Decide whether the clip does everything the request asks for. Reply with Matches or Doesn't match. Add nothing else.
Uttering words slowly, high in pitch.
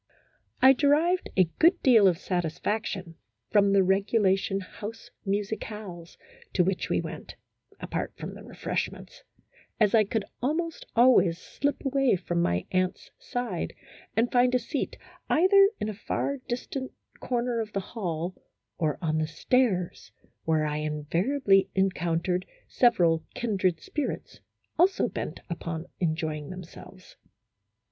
Matches